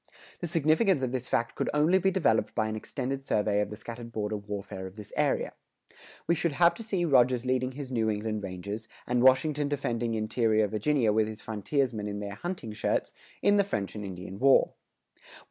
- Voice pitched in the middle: No, low, 115 Hz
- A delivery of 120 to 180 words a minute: No, average, 195 wpm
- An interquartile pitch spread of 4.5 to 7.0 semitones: Yes, average, 5.3 semitones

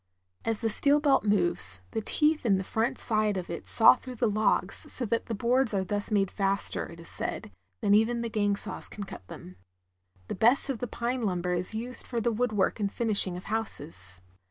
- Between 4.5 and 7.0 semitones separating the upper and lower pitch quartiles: No, average, 3.8 semitones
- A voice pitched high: Yes, high, 215 Hz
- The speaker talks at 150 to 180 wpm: No, fast, 205 wpm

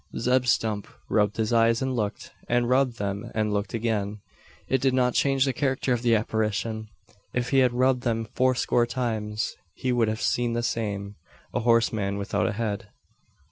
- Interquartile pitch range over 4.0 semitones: No, average, 2.7 semitones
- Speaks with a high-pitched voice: No, low, 115 Hz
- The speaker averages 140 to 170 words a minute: No, average, 180 wpm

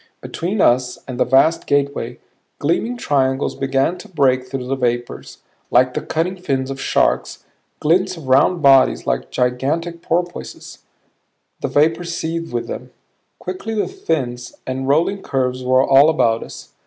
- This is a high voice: No, medium, 140 Hz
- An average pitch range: Yes, average, 4.5 semitones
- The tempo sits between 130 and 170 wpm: Yes, average, 150 wpm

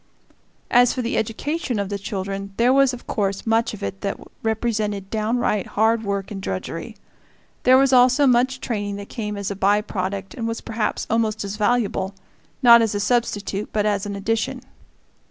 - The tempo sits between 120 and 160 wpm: No, average, 180 wpm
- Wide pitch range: No, average, 2.9 semitones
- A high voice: Yes, high, 215 Hz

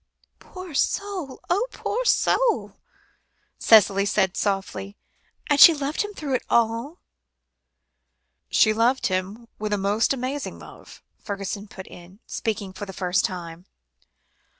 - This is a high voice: Yes, high, 215 Hz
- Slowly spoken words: Yes, slow, 125 wpm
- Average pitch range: No, wide, 6.4 semitones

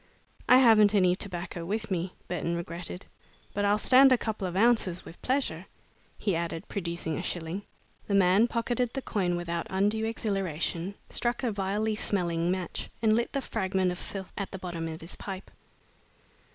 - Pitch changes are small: No, average, 3.9 semitones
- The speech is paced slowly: No, average, 170 wpm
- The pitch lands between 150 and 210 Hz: Yes, high, 190 Hz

